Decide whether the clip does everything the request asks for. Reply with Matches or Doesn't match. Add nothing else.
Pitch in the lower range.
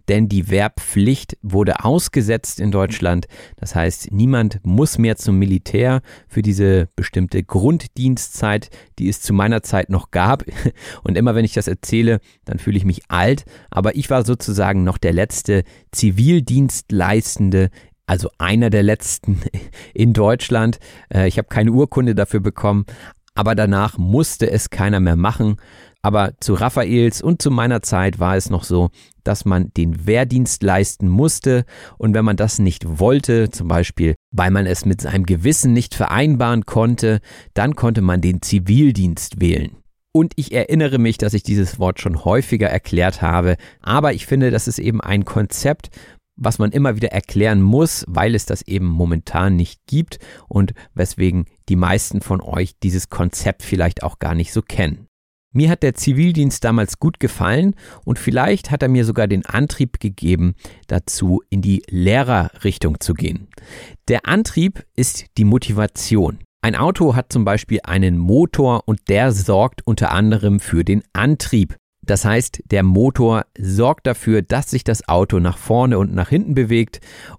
Matches